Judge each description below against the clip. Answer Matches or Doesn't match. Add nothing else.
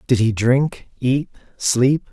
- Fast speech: Doesn't match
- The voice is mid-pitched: Doesn't match